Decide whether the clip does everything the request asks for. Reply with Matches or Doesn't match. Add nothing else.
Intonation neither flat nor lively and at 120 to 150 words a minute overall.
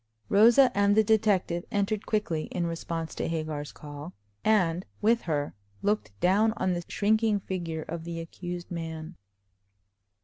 Matches